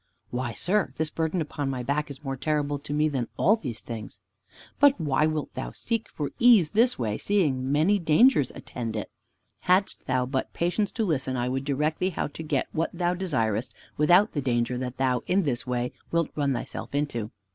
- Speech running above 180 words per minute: Yes, average, 200 wpm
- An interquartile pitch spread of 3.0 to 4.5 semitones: No, average, 5.2 semitones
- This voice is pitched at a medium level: Yes, medium, 145 Hz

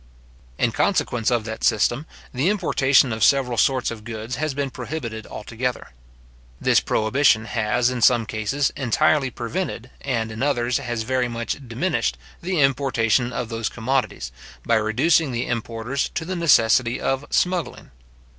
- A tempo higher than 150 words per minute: No, average, 145 wpm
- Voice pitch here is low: Yes, low, 125 Hz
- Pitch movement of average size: Yes, average, 3.4 semitones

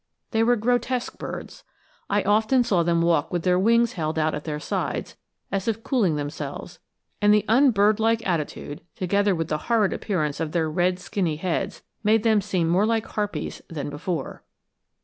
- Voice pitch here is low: No, high, 190 Hz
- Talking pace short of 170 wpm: No, average, 175 wpm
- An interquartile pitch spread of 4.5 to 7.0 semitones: Yes, average, 5.1 semitones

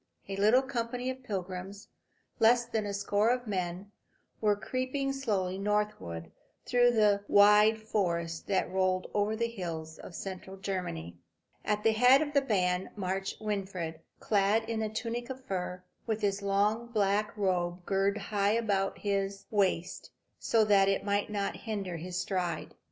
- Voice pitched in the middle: No, high, 205 Hz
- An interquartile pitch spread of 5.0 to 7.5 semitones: No, average, 2.8 semitones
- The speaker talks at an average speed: Yes, average, 155 wpm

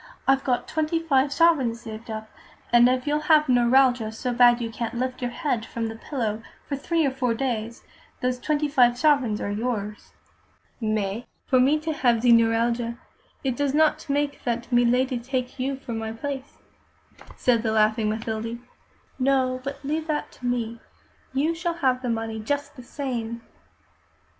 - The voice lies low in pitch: No, very high, 250 Hz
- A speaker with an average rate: Yes, average, 170 wpm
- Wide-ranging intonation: No, average, 3.3 semitones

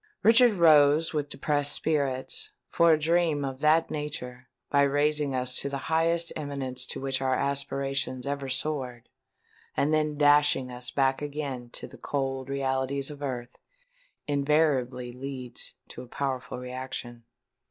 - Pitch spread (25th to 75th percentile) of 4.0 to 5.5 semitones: No, narrow, 2.6 semitones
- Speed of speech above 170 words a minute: No, slow, 135 wpm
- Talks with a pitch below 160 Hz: Yes, medium, 140 Hz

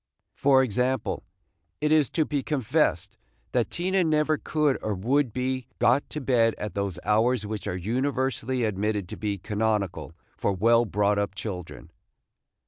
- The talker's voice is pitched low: Yes, low, 115 Hz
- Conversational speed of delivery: Yes, average, 150 wpm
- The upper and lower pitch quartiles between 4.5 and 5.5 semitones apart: Yes, average, 4.8 semitones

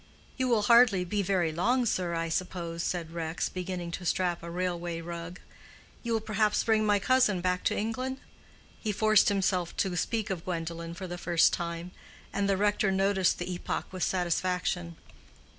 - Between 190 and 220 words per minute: No, average, 175 wpm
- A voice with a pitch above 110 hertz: Yes, medium, 185 Hz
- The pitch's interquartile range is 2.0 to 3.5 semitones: Yes, average, 3.2 semitones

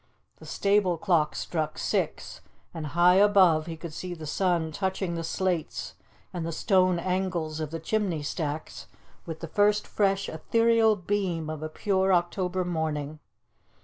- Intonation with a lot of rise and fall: No, average, 3.2 semitones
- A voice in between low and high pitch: Yes, medium, 175 Hz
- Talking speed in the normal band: Yes, average, 150 wpm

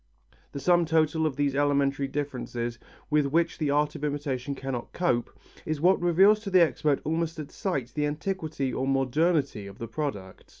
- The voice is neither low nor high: Yes, medium, 145 Hz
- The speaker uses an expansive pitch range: No, average, 3.3 semitones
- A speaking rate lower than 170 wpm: No, average, 175 wpm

